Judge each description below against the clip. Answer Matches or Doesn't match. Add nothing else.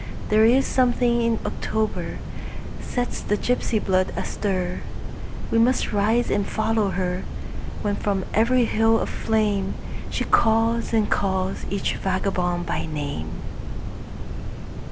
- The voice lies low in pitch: Doesn't match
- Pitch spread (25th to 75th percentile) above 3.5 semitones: Doesn't match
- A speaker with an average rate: Doesn't match